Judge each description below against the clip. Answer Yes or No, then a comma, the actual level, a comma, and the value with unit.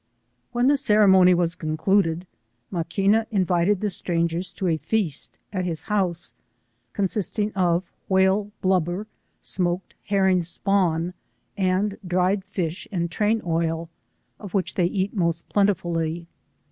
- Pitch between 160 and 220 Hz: Yes, medium, 185 Hz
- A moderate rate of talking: No, slow, 125 wpm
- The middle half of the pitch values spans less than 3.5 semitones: Yes, average, 2.9 semitones